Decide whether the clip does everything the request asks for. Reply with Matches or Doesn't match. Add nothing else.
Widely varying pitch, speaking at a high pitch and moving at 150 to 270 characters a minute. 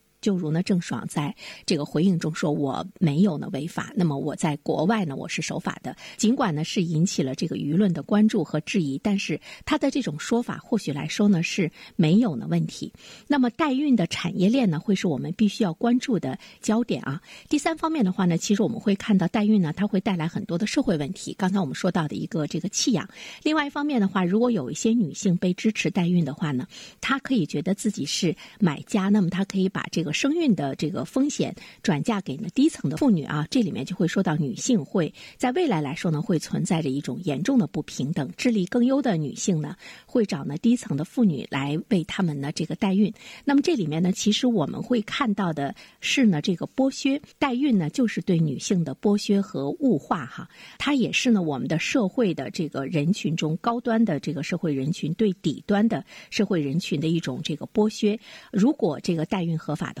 Doesn't match